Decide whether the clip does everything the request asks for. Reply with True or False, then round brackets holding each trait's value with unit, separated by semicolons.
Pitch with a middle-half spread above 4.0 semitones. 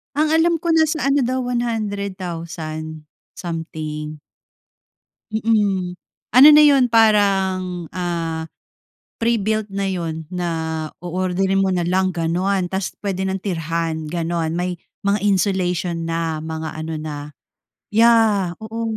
True (4.4 semitones)